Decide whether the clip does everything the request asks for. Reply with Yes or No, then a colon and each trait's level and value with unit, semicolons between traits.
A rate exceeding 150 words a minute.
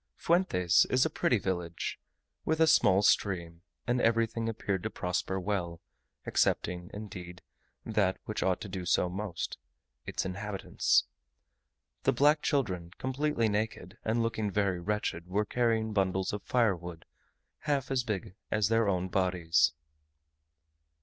No: slow, 135 wpm